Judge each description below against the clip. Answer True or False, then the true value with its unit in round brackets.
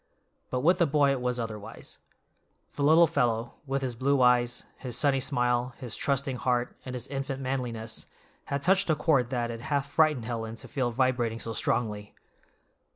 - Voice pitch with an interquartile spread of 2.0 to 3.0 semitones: True (2.7 semitones)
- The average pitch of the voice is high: False (125 Hz)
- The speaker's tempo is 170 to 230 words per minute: True (175 wpm)